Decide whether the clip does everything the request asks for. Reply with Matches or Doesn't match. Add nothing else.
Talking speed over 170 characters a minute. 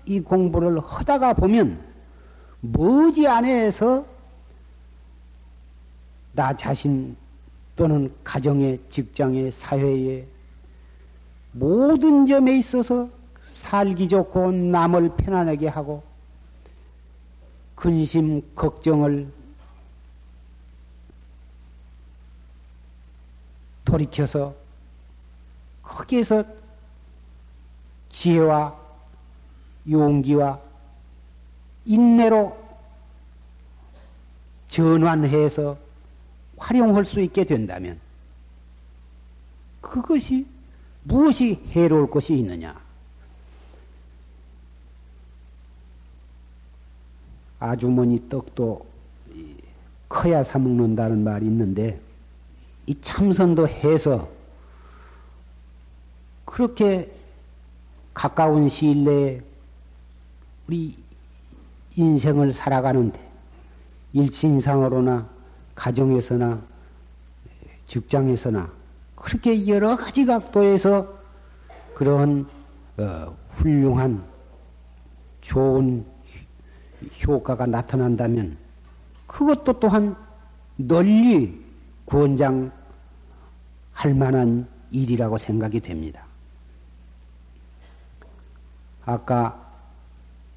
Doesn't match